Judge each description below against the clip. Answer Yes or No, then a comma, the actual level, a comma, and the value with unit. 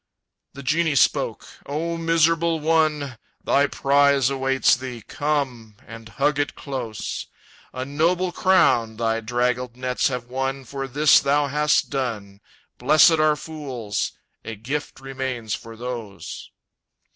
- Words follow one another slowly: Yes, slow, 130 wpm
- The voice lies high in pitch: No, low, 135 Hz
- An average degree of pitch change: Yes, average, 3.7 semitones